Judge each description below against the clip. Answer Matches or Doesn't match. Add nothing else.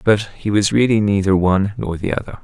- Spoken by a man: Matches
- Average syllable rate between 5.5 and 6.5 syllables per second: Matches